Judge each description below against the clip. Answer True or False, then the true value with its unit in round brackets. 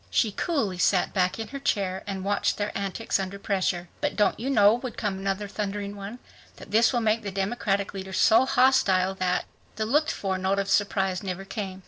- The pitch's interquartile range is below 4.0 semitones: True (2.6 semitones)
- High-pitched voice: True (200 Hz)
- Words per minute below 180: False (205 wpm)